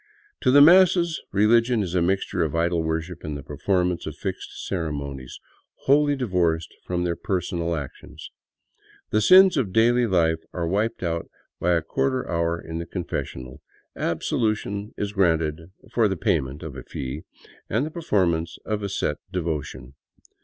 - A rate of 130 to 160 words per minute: Yes, average, 155 wpm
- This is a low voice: Yes, very low, 90 Hz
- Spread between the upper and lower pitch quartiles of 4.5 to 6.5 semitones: Yes, average, 5.0 semitones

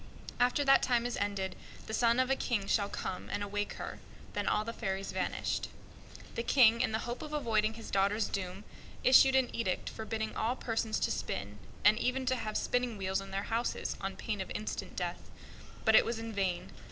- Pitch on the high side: Yes, high, 220 Hz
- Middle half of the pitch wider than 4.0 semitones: No, average, 3.4 semitones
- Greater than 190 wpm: Yes, average, 200 wpm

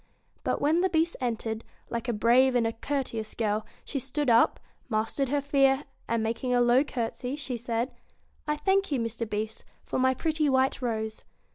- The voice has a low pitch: No, high, 245 Hz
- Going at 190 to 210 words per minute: No, average, 180 wpm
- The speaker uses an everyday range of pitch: Yes, average, 3.6 semitones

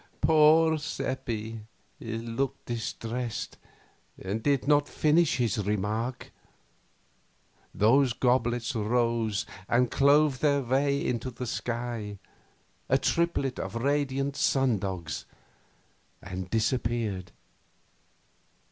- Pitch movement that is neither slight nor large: Yes, average, 3.8 semitones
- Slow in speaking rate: Yes, slow, 85 wpm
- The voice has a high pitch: No, low, 120 Hz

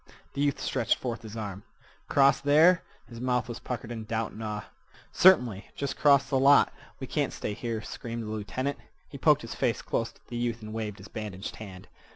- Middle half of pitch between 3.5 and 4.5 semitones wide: Yes, average, 3.9 semitones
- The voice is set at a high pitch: No, low, 115 Hz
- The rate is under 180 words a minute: No, average, 200 wpm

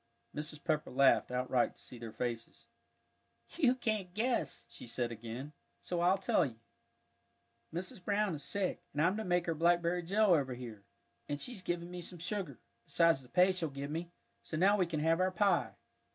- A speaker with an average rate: Yes, average, 185 wpm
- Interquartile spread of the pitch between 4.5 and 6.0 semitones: Yes, average, 5.0 semitones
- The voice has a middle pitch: Yes, medium, 170 Hz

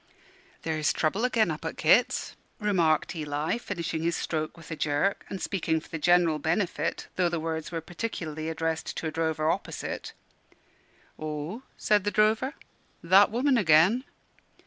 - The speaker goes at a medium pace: Yes, average, 150 wpm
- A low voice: No, medium, 165 Hz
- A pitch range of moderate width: Yes, average, 4.3 semitones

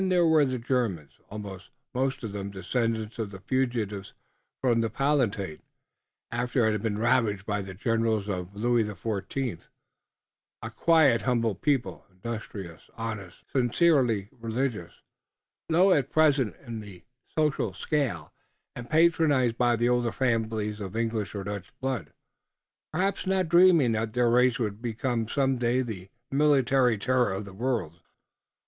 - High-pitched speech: No, low, 115 Hz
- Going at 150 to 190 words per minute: No, average, 140 wpm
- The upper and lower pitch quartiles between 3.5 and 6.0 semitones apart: Yes, average, 4.2 semitones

